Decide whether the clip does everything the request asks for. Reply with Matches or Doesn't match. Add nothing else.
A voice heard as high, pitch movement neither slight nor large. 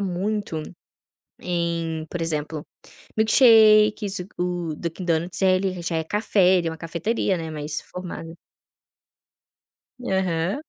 Doesn't match